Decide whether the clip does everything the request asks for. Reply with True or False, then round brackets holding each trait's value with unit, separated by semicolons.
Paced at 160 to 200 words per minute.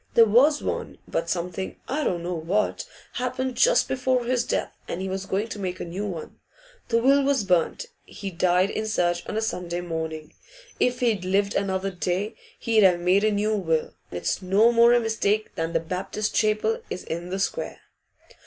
True (190 wpm)